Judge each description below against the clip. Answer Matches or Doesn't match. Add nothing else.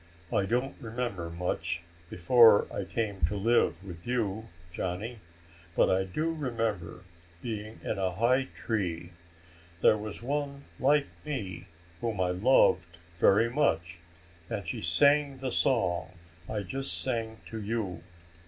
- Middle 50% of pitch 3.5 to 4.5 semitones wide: Doesn't match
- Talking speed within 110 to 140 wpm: Matches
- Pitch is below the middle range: Matches